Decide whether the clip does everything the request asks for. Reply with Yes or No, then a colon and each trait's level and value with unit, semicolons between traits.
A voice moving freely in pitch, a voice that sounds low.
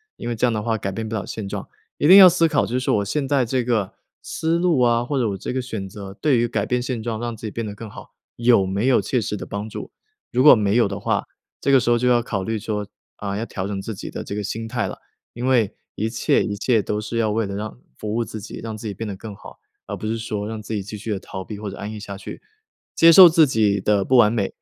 No: average, 3.0 semitones; low, 110 Hz